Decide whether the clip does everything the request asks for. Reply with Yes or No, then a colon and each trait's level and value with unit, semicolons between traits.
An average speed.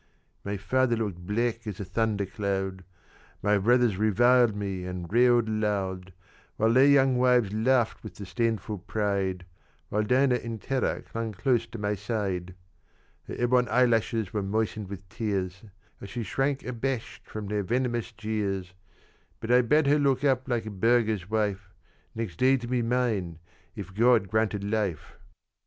Yes: average, 155 wpm